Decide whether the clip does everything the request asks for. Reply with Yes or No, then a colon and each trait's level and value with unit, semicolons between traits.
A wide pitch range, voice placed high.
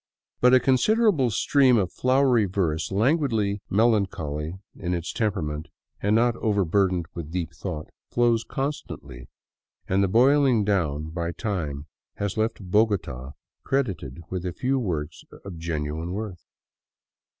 No: wide, 6.3 semitones; low, 100 Hz